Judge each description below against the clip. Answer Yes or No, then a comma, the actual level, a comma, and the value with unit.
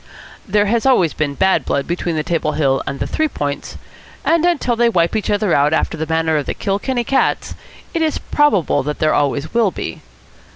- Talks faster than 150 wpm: Yes, fast, 205 wpm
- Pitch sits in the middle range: Yes, medium, 175 Hz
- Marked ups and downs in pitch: Yes, wide, 7.5 semitones